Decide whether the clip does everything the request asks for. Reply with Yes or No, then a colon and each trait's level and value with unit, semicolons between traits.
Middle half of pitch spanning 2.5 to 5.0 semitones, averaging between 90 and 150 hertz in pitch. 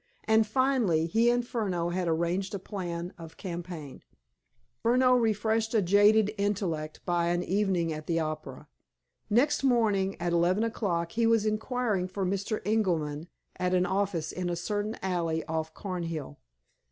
No: average, 4.3 semitones; high, 190 Hz